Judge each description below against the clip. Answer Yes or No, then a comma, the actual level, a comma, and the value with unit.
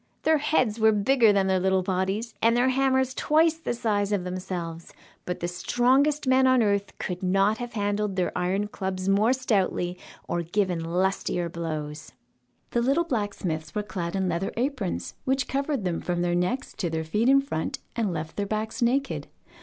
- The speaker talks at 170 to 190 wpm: Yes, average, 180 wpm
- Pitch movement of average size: No, wide, 5.7 semitones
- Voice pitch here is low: No, high, 205 Hz